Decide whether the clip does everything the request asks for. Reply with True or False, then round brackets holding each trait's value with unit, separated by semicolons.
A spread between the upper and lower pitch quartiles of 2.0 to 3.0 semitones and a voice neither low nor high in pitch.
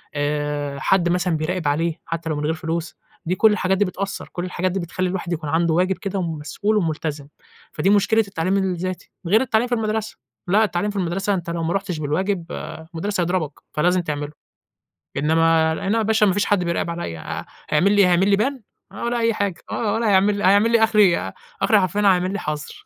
False (3.8 semitones; 180 Hz)